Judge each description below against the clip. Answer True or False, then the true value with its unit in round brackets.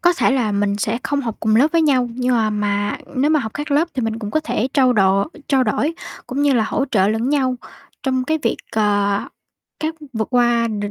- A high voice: True (240 Hz)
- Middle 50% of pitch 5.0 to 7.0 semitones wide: False (4.6 semitones)